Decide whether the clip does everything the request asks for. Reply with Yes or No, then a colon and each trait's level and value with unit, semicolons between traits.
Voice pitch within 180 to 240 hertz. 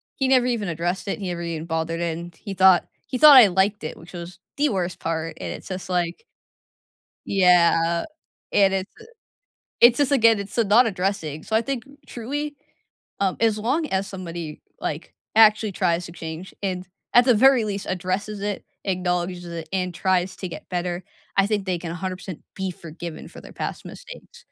Yes: high, 190 Hz